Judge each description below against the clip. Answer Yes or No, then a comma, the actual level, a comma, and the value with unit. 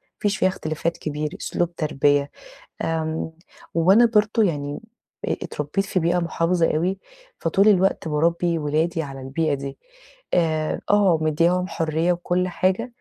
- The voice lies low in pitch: No, medium, 165 Hz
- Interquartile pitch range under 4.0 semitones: Yes, average, 2.9 semitones